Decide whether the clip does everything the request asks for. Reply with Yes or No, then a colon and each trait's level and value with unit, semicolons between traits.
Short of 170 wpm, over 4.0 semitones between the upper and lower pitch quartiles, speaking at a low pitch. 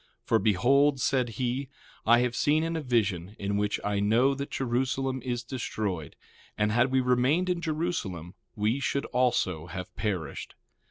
Yes: average, 160 wpm; average, 4.6 semitones; low, 120 Hz